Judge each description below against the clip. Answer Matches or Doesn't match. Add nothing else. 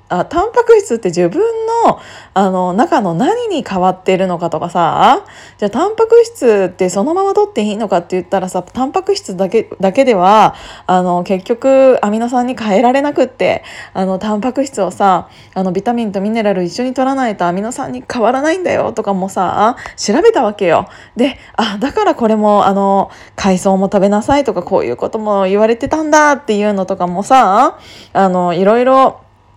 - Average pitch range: Doesn't match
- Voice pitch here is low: Doesn't match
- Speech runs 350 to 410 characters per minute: Matches